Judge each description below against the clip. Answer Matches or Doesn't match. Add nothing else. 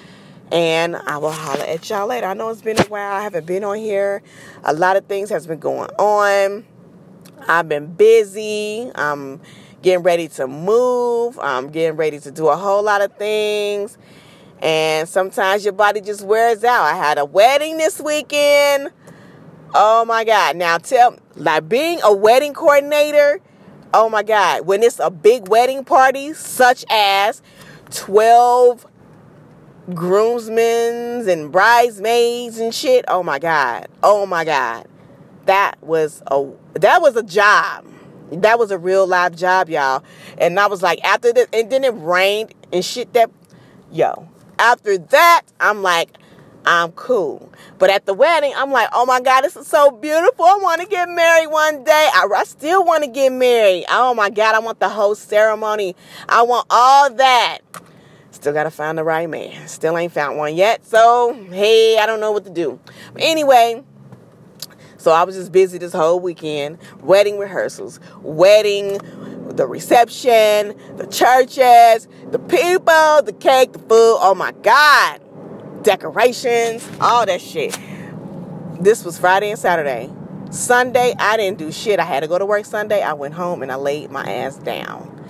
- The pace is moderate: Matches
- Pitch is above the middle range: Matches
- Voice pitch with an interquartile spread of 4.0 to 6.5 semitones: Matches